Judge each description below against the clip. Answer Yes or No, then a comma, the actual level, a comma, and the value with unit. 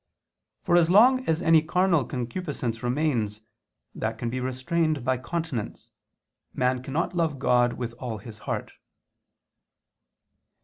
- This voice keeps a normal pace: No, slow, 125 wpm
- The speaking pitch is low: Yes, low, 130 Hz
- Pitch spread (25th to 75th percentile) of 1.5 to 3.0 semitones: No, average, 5.3 semitones